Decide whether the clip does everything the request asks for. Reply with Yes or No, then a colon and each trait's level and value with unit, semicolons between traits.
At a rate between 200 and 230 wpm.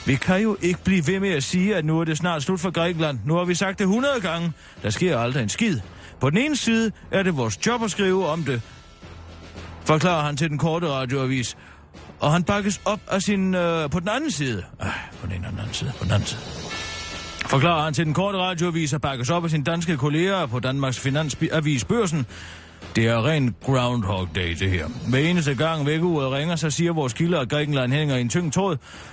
Yes: average, 220 wpm